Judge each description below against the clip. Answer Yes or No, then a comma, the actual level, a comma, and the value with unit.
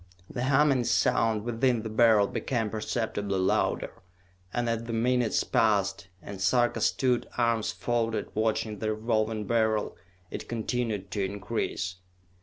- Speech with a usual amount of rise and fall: No, narrow, 2.2 semitones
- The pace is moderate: No, slow, 130 wpm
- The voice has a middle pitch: No, low, 115 Hz